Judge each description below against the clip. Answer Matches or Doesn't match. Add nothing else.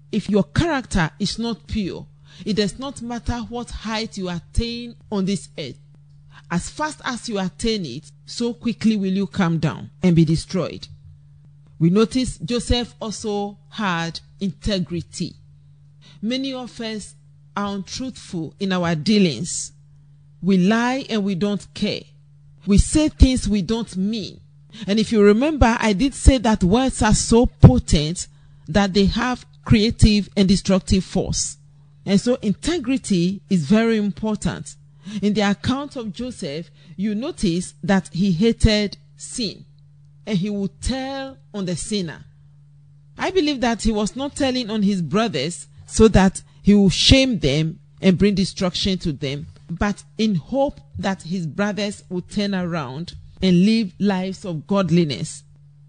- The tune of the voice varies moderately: Doesn't match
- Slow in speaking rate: Doesn't match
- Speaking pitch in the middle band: Doesn't match